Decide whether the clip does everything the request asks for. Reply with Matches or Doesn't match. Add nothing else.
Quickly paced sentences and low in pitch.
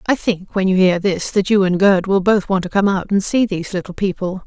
Doesn't match